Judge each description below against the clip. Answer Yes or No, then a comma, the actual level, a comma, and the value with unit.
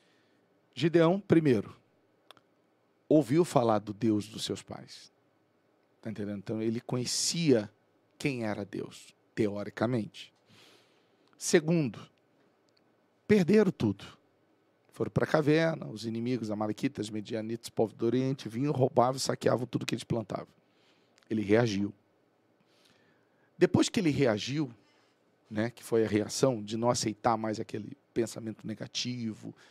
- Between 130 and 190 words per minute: No, slow, 120 wpm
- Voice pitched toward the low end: Yes, low, 115 Hz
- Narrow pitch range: No, average, 4.3 semitones